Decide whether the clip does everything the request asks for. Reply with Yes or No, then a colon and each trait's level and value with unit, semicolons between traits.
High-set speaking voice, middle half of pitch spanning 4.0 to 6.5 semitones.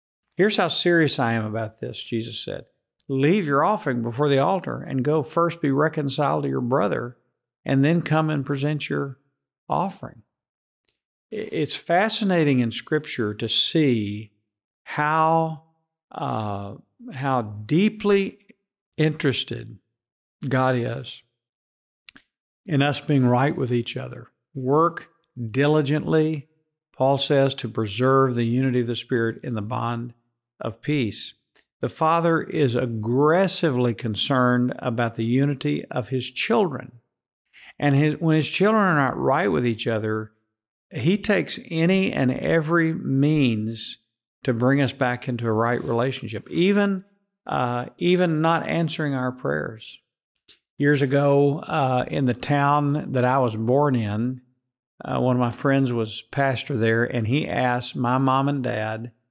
No: low, 135 Hz; average, 4.5 semitones